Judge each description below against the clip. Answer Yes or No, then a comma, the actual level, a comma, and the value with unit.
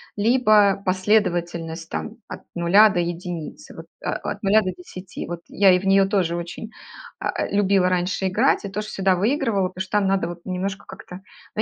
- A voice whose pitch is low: No, high, 190 Hz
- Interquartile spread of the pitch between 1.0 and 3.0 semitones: Yes, average, 2.7 semitones